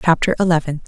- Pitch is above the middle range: No, medium, 165 Hz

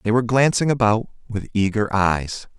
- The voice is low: Yes, low, 110 Hz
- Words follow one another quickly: No, average, 160 wpm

